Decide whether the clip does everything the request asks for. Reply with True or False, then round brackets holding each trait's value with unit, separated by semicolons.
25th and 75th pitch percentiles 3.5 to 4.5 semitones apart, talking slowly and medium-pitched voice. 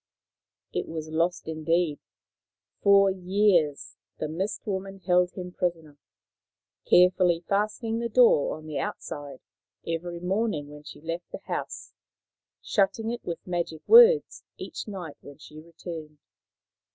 True (3.9 semitones; 125 wpm; 175 Hz)